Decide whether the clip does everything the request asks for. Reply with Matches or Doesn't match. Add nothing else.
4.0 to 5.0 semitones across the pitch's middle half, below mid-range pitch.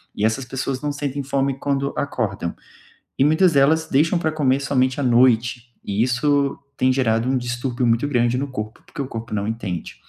Doesn't match